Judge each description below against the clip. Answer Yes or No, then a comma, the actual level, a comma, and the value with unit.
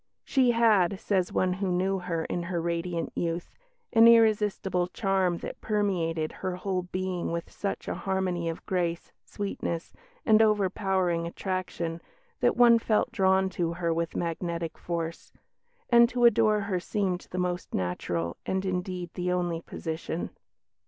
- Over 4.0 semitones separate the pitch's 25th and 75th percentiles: No, average, 2.7 semitones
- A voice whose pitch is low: No, medium, 180 Hz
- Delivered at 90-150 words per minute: Yes, average, 145 wpm